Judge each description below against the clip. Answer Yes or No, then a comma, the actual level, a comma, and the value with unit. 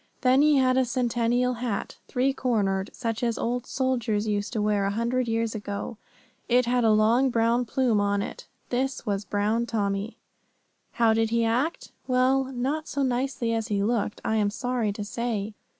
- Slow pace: No, average, 180 wpm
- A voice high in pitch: Yes, high, 235 Hz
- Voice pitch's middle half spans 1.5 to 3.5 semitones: Yes, average, 3.0 semitones